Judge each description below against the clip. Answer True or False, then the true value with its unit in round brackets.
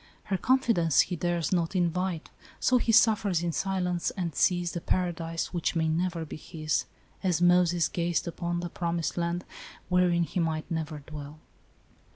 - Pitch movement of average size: False (1.6 semitones)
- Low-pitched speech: False (175 Hz)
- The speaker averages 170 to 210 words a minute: False (160 wpm)